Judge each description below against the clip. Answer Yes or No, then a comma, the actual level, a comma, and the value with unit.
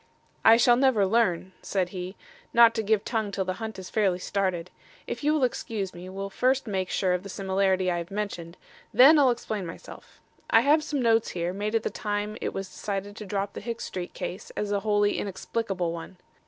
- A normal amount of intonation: Yes, average, 3.3 semitones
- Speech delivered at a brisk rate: Yes, fast, 210 wpm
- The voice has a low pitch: No, high, 200 Hz